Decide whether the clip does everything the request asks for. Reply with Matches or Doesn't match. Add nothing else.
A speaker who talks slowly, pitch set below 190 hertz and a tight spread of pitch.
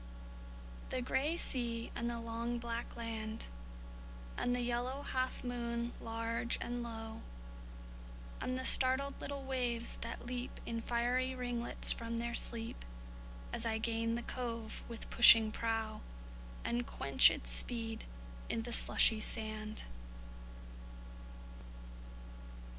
Doesn't match